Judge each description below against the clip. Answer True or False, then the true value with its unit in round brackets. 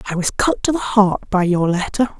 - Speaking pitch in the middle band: False (205 Hz)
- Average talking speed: False (245 wpm)